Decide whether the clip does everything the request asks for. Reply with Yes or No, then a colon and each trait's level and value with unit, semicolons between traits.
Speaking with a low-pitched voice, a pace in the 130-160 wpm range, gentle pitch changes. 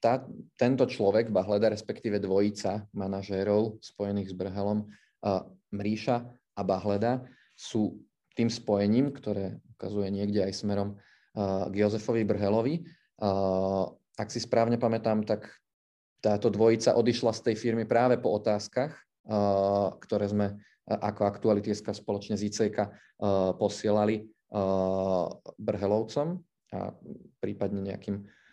No: low, 105 Hz; average, 120 wpm; narrow, 2.2 semitones